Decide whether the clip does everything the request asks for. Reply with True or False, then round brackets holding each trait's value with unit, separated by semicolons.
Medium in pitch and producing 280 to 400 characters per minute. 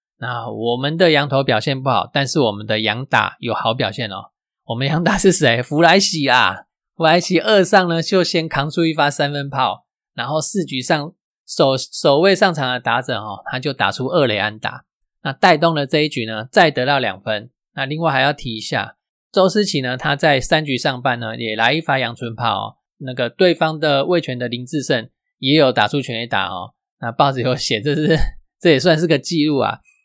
True (145 Hz; 285 characters per minute)